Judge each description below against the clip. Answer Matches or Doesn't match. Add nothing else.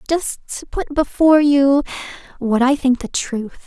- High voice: Matches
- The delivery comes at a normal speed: Matches